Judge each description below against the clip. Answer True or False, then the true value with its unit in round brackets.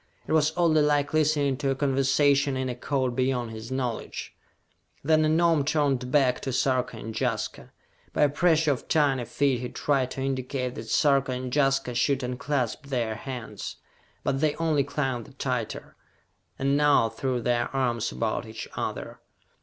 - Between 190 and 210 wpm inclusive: False (170 wpm)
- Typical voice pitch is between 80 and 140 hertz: True (135 Hz)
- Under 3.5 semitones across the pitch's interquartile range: True (2.6 semitones)